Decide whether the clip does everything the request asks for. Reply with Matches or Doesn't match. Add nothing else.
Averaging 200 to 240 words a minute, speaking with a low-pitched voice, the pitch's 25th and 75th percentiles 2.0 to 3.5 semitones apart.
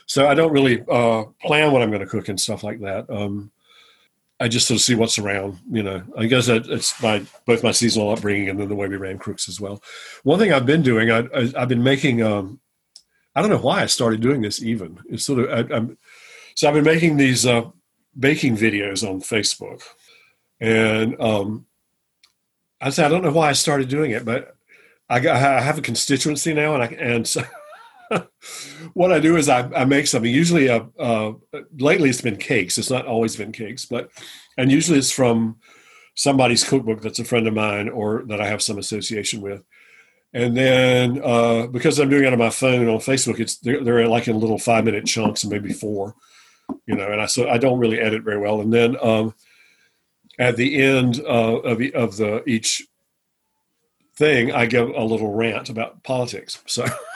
Matches